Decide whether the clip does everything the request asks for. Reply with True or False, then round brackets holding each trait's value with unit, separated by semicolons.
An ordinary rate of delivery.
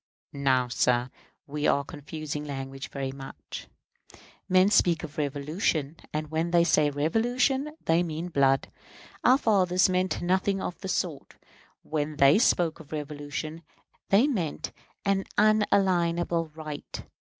False (130 wpm)